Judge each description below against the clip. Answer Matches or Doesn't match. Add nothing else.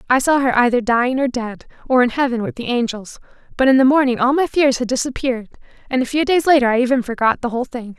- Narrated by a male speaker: Doesn't match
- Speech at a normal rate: Doesn't match